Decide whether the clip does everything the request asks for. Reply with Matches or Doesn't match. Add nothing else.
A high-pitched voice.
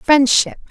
Matches